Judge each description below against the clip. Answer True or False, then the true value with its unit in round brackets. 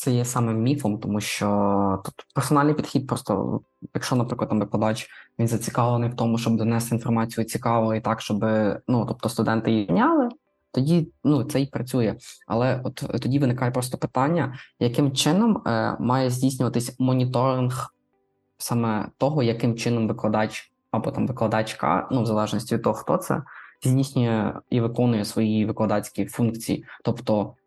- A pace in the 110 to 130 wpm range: False (150 wpm)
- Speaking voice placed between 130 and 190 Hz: False (120 Hz)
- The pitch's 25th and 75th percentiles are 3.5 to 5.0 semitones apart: False (3.0 semitones)